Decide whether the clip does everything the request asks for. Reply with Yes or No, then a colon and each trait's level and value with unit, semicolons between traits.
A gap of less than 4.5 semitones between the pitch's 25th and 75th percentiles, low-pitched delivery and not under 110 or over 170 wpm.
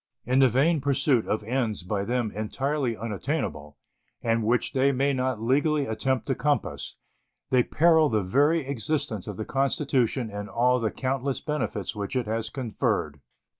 Yes: average, 4.1 semitones; low, 125 Hz; average, 160 wpm